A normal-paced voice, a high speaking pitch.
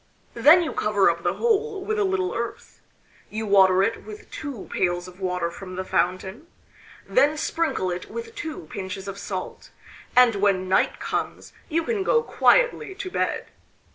Yes: average, 170 wpm; high, 220 Hz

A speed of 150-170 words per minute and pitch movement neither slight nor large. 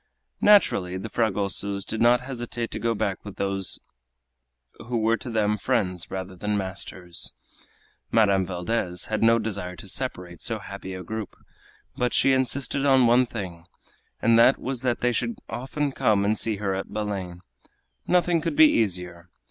Yes: average, 165 wpm; average, 4.1 semitones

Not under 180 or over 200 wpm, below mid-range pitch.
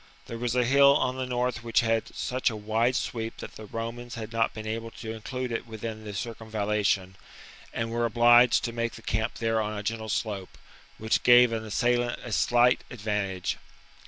Yes: average, 190 wpm; low, 115 Hz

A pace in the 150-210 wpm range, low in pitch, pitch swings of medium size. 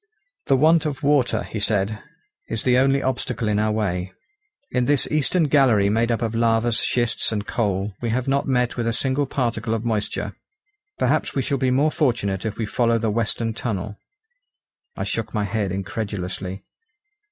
Yes: average, 175 wpm; low, 115 Hz; average, 3.6 semitones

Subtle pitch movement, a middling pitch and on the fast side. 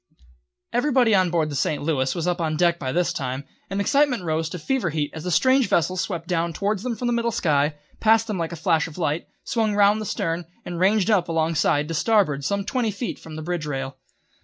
No: average, 5.3 semitones; medium, 175 Hz; fast, 235 wpm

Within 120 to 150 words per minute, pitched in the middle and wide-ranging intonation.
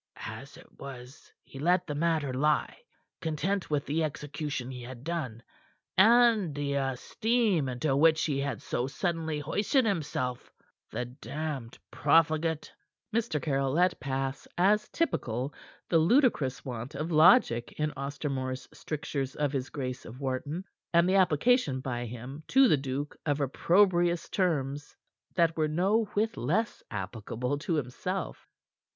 No: average, 140 wpm; medium, 150 Hz; average, 4.5 semitones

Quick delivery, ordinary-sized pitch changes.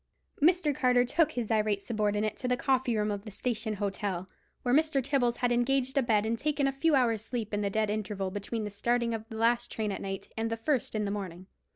Yes: fast, 235 wpm; average, 3.3 semitones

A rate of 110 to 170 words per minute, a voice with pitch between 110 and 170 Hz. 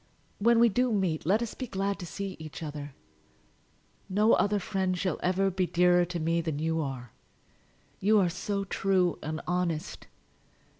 No: average, 165 wpm; medium, 180 Hz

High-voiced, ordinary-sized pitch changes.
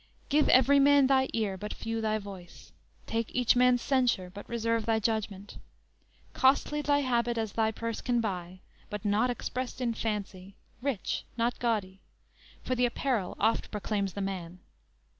Yes: high, 225 Hz; average, 3.6 semitones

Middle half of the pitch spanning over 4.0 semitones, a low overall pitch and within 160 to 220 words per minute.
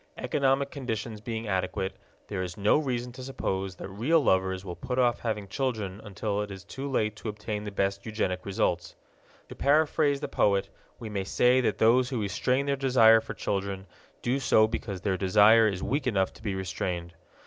Yes: average, 4.4 semitones; low, 105 Hz; average, 190 wpm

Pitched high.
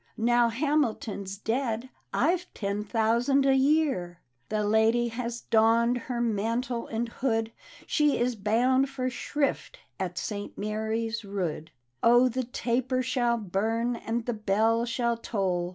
Yes: high, 230 Hz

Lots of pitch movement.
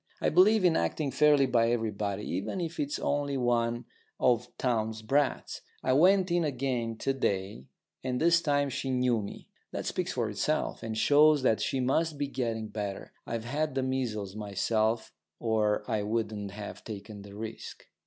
No: average, 4.7 semitones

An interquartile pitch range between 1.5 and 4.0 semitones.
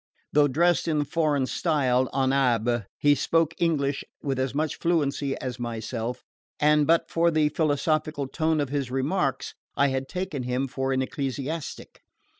Yes: average, 2.9 semitones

